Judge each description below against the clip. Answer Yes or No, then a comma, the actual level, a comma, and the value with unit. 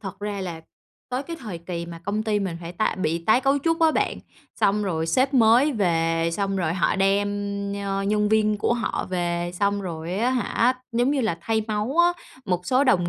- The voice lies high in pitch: Yes, high, 205 Hz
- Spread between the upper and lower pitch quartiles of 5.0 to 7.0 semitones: Yes, wide, 5.4 semitones